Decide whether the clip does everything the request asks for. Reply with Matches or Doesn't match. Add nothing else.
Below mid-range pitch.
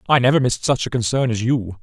Matches